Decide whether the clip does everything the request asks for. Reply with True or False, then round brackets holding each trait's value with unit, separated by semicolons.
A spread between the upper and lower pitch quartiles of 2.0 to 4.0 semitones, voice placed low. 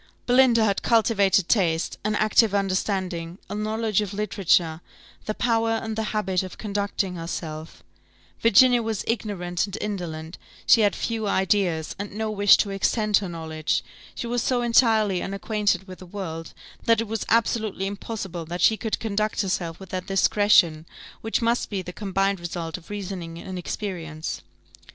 False (3.4 semitones; 200 Hz)